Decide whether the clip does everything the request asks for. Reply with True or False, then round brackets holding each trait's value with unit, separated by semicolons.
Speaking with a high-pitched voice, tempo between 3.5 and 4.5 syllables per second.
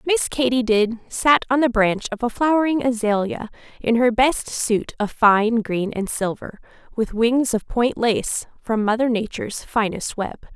True (235 Hz; 4.3 syllables/s)